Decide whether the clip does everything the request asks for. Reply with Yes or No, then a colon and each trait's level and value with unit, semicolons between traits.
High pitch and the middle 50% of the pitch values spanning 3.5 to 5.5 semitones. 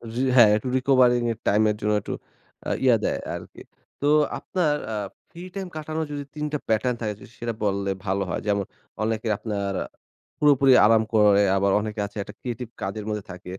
No: low, 110 Hz; average, 4.0 semitones